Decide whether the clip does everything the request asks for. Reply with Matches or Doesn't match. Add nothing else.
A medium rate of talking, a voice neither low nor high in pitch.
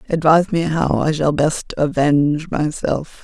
Matches